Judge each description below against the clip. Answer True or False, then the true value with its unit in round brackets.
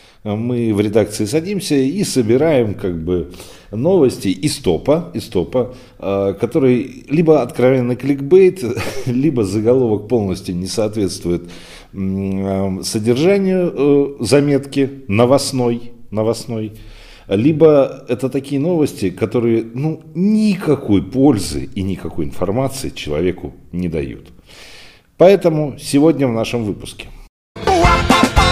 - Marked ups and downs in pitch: True (6.1 semitones)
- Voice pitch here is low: True (120 Hz)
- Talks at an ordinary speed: False (100 wpm)